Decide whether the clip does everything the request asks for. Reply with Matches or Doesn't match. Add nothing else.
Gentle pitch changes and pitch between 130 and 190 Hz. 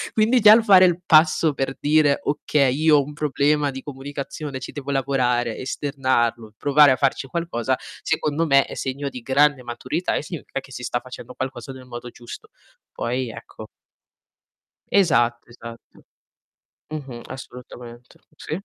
Doesn't match